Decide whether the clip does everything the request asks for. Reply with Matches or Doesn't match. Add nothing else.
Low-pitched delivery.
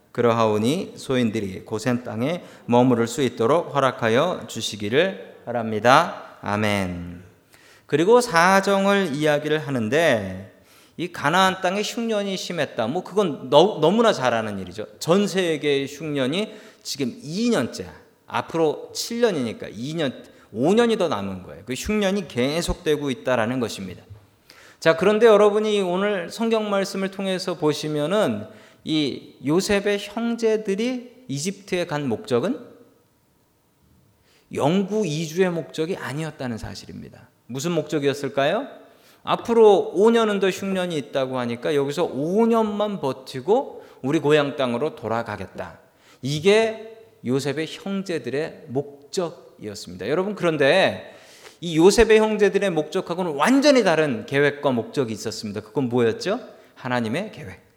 Doesn't match